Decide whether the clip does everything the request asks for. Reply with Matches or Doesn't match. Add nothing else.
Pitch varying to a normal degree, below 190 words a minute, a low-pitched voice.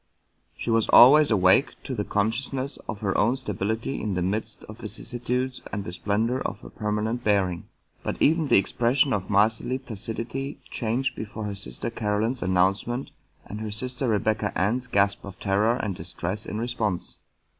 Matches